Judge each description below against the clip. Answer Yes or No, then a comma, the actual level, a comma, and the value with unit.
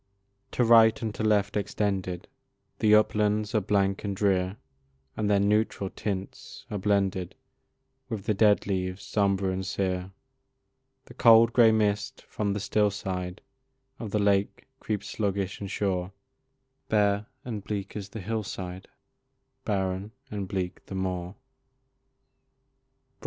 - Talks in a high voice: No, low, 100 Hz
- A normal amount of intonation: No, narrow, 1.9 semitones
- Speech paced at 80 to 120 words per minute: No, slow, 135 wpm